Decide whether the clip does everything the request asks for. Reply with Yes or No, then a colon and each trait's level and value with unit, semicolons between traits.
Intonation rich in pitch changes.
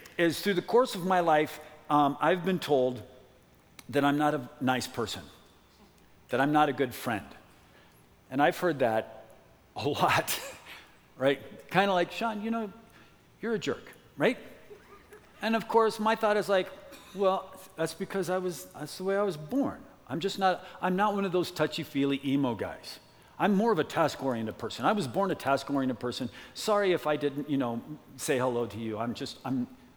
Yes: wide, 6.9 semitones